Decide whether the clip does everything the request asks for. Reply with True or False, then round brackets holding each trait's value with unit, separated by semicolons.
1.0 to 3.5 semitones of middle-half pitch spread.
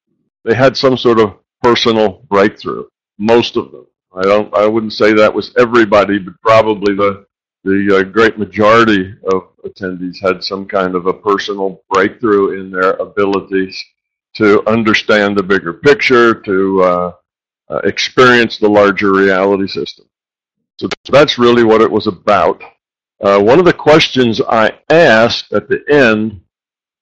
True (3.0 semitones)